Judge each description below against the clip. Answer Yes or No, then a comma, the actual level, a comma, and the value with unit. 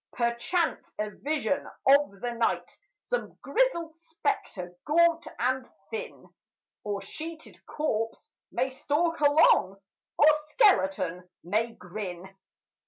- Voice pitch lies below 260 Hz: No, very high, 275 Hz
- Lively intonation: Yes, wide, 7.5 semitones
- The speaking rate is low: Yes, slow, 105 wpm